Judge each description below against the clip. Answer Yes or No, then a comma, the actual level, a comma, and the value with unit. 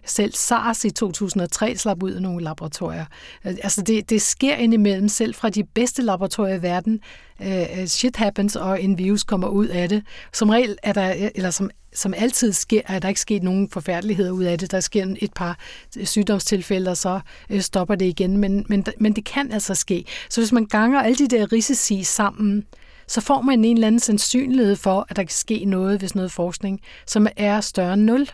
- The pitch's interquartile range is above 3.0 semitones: No, average, 2.7 semitones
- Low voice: No, high, 205 Hz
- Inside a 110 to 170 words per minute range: No, average, 200 wpm